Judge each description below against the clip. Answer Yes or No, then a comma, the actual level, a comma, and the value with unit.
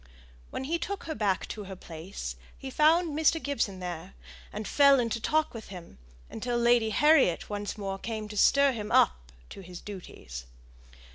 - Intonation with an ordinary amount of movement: No, wide, 7.0 semitones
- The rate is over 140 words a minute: Yes, average, 170 wpm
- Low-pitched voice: No, high, 215 Hz